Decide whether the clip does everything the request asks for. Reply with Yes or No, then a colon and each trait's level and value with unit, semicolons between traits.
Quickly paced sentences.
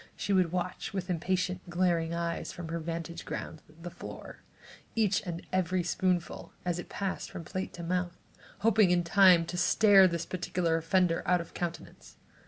No: average, 175 wpm